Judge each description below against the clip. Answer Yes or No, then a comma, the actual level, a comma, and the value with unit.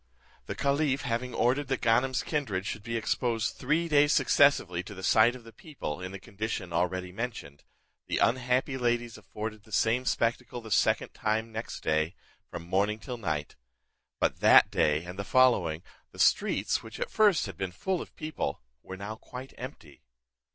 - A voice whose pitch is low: Yes, low, 115 Hz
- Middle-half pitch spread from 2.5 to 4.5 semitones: No, average, 5.3 semitones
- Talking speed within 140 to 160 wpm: No, average, 175 wpm